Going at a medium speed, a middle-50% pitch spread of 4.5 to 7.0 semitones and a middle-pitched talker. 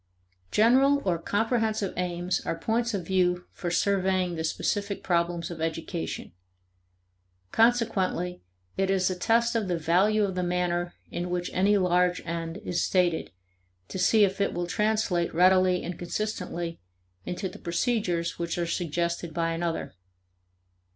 No: average, 145 wpm; average, 2.7 semitones; medium, 180 Hz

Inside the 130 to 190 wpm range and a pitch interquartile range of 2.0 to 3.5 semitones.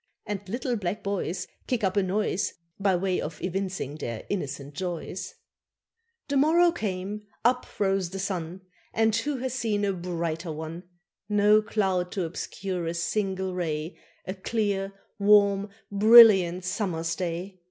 Yes: average, 140 wpm; average, 3.0 semitones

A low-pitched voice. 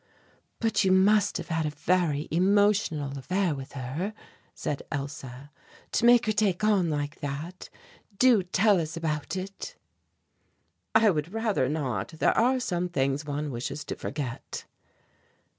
No: medium, 165 Hz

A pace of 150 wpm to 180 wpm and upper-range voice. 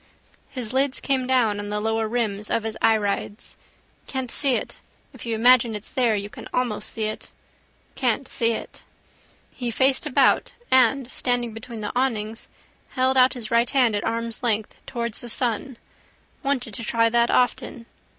Yes: average, 170 wpm; high, 235 Hz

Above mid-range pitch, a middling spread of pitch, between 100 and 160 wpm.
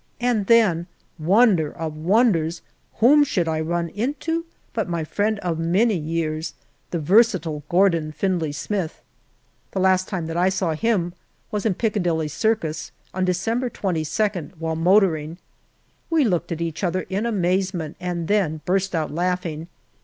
No: medium, 180 Hz; average, 4.2 semitones; average, 145 wpm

